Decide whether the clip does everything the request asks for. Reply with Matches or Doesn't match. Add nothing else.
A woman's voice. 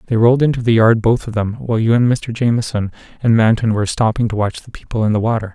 Doesn't match